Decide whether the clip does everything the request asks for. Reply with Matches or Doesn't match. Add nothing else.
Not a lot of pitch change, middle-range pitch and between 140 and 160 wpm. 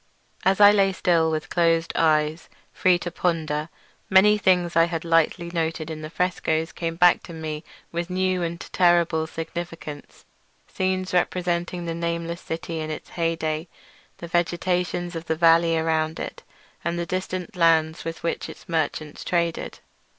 Matches